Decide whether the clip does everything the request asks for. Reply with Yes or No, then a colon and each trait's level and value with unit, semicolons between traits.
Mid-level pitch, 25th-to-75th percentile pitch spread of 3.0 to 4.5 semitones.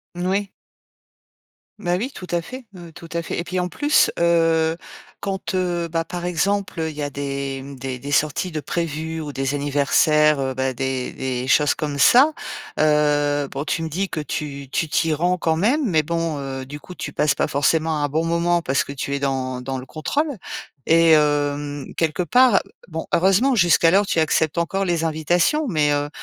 Yes: medium, 160 Hz; average, 3.4 semitones